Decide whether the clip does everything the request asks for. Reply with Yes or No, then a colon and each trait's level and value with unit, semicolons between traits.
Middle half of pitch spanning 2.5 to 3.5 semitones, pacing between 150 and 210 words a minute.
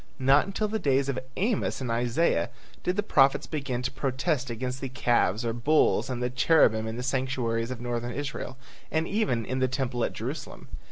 Yes: average, 2.8 semitones; average, 190 wpm